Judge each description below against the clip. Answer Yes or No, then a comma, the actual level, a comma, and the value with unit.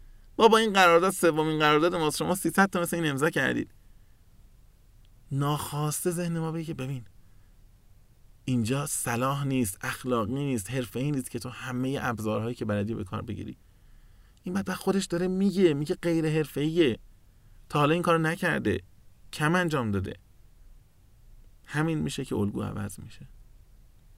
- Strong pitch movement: Yes, wide, 7.3 semitones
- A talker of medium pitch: No, low, 130 Hz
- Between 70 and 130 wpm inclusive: No, average, 145 wpm